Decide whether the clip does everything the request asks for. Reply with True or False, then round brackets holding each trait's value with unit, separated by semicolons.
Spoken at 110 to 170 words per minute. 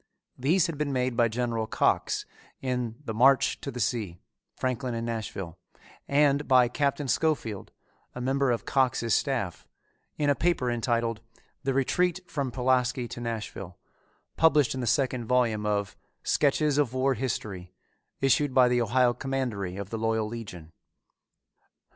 True (150 wpm)